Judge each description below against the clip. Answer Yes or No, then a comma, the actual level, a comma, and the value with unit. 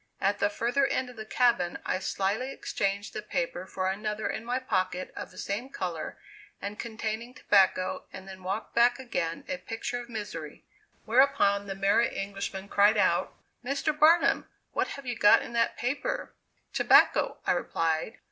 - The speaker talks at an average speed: Yes, average, 165 wpm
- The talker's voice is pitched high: Yes, high, 210 Hz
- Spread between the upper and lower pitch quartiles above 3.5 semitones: Yes, average, 4.0 semitones